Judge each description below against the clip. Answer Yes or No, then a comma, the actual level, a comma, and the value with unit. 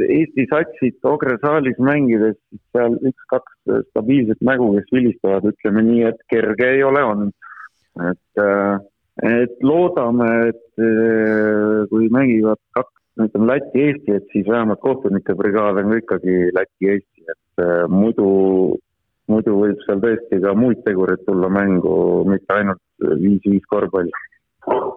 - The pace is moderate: No, slow, 125 wpm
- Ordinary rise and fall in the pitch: Yes, average, 3.1 semitones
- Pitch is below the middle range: Yes, low, 110 Hz